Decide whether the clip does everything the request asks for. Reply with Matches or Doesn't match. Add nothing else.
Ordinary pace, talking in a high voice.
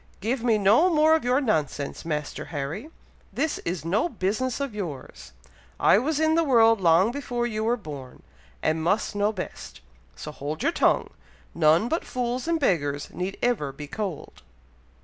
Matches